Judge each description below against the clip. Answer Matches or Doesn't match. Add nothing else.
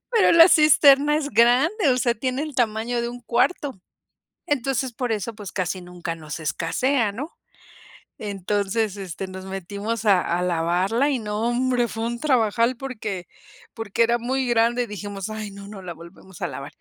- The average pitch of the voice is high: Matches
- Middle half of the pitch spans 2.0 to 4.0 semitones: Doesn't match